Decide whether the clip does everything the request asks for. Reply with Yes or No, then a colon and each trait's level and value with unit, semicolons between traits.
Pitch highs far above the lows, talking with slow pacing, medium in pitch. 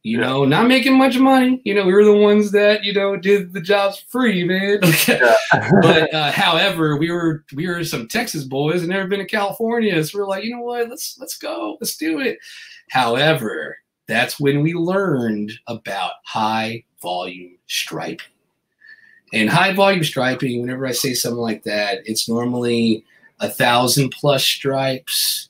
No: wide, 8.0 semitones; average, 170 wpm; medium, 175 Hz